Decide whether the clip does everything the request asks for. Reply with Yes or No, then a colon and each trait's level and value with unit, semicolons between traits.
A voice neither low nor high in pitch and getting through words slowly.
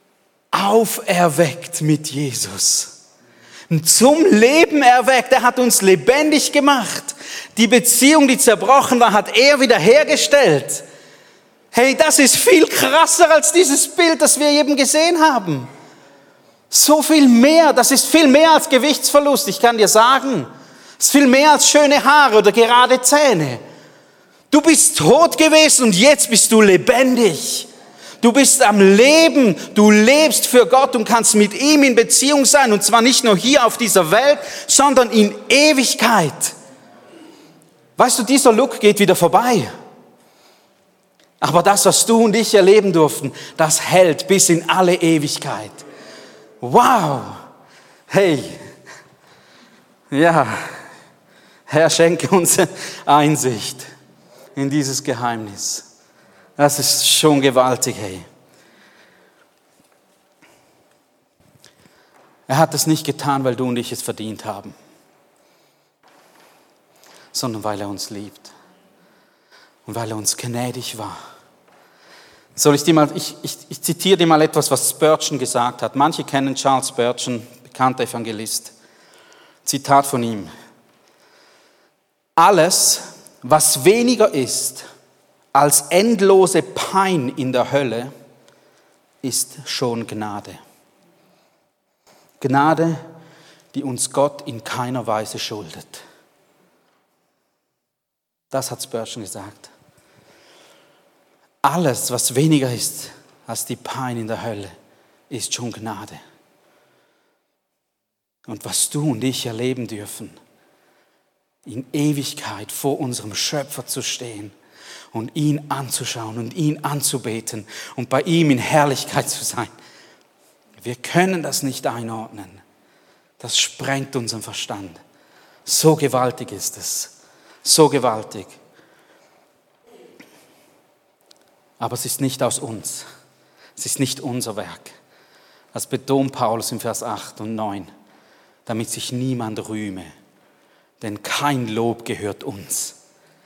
Yes: medium, 150 Hz; slow, 120 wpm